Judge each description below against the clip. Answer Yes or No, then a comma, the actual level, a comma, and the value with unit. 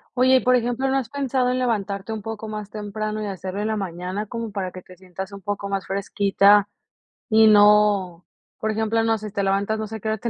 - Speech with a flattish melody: Yes, narrow, 2.1 semitones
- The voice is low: No, high, 210 Hz